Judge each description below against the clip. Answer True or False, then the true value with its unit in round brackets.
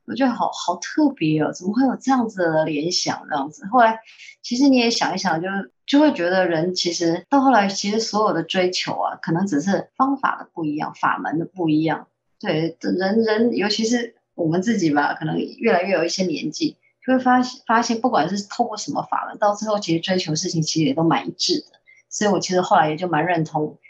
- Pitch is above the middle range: True (195 Hz)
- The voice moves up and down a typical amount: False (6.4 semitones)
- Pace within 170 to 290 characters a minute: False (325 characters per minute)